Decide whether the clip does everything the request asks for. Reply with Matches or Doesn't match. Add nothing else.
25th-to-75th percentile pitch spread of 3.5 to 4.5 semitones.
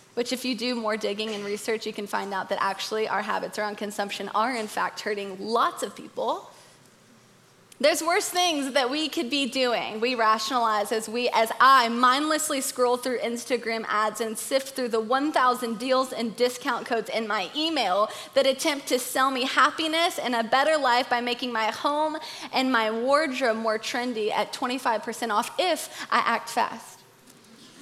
Matches